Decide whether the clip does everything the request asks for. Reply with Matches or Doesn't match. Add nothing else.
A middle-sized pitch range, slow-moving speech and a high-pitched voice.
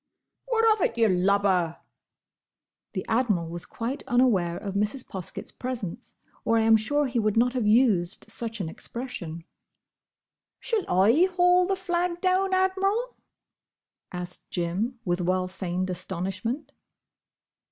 Doesn't match